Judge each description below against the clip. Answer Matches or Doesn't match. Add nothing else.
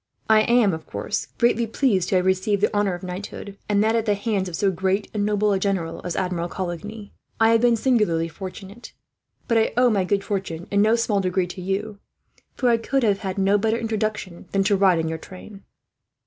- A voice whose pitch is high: Matches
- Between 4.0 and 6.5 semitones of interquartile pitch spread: Doesn't match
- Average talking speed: Doesn't match